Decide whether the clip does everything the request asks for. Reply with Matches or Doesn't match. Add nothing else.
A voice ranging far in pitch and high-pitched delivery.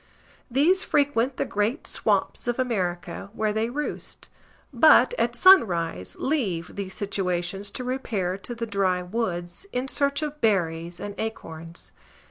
Matches